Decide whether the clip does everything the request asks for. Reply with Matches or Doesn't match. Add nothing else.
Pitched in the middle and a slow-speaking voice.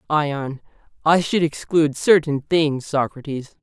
Matches